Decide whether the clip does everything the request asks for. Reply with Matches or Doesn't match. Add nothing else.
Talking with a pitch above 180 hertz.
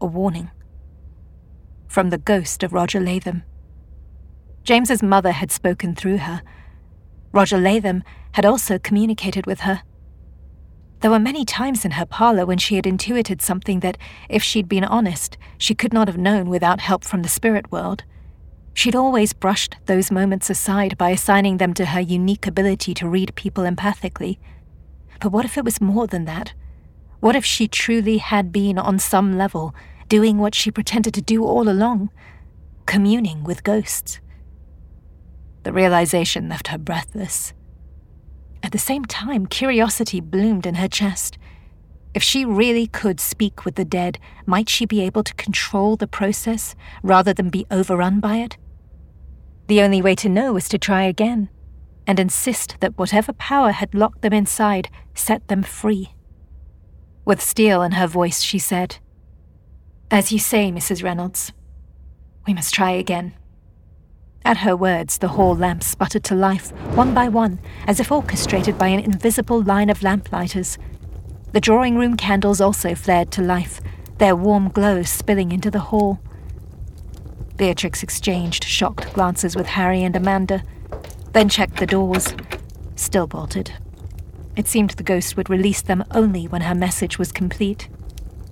Matches